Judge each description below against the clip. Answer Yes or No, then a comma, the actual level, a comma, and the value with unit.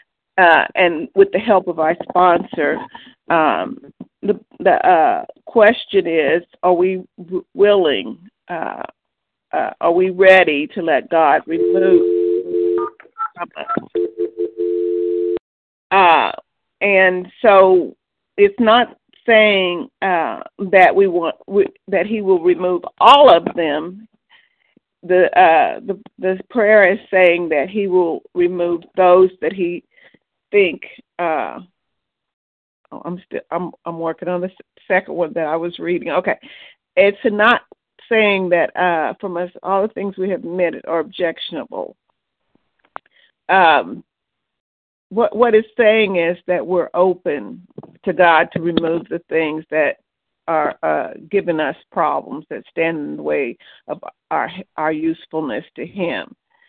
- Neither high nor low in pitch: Yes, medium, 180 Hz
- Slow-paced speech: Yes, slow, 130 wpm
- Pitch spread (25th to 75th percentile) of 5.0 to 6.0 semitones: No, average, 4.0 semitones